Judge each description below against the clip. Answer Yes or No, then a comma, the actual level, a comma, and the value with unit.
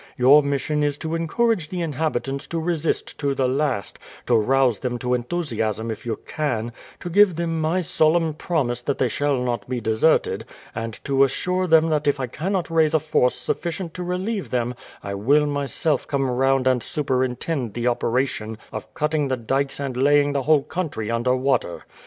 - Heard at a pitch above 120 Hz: Yes, medium, 140 Hz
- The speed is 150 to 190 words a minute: Yes, average, 180 wpm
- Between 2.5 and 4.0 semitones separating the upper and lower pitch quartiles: No, average, 4.4 semitones